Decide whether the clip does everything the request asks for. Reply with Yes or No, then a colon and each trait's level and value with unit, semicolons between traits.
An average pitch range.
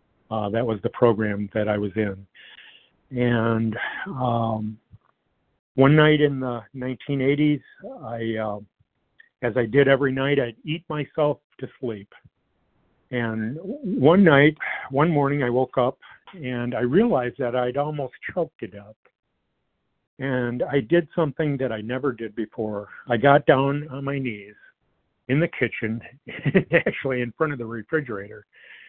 Yes: average, 4.2 semitones